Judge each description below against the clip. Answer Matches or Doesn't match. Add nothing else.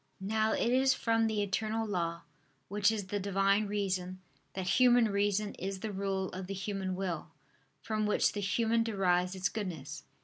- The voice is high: Matches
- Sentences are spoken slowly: Doesn't match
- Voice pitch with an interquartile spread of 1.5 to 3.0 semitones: Matches